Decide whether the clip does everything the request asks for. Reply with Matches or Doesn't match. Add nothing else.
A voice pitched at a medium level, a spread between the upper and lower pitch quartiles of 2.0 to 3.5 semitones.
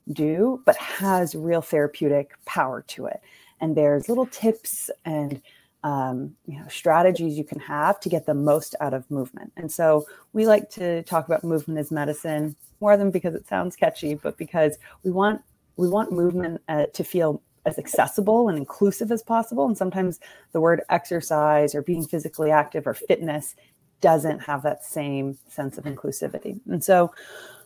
Doesn't match